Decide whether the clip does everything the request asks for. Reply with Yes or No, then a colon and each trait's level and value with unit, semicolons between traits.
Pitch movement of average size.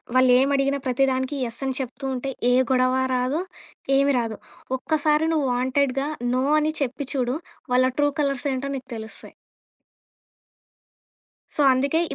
No: narrow, 1.9 semitones